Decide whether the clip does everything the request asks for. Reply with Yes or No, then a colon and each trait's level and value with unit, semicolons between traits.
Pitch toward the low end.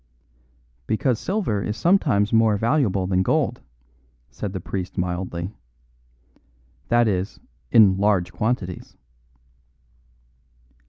Yes: low, 100 Hz